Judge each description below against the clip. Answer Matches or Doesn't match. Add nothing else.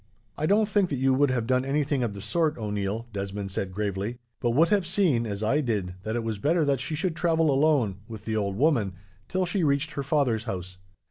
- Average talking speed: Doesn't match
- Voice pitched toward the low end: Matches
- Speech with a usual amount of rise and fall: Doesn't match